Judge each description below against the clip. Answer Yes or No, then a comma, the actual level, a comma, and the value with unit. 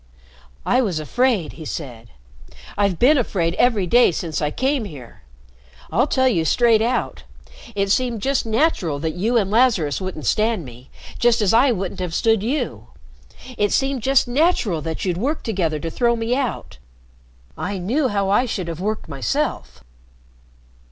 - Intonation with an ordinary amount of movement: No, wide, 6.6 semitones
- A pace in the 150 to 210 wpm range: Yes, average, 165 wpm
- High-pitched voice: Yes, high, 205 Hz